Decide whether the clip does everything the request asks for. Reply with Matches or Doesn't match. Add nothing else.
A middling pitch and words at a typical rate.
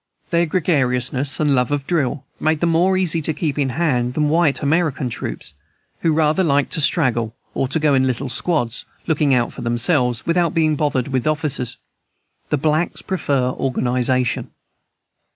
Matches